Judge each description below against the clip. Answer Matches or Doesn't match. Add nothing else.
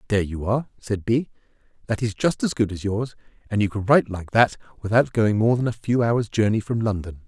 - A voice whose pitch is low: Matches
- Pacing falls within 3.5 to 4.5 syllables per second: Doesn't match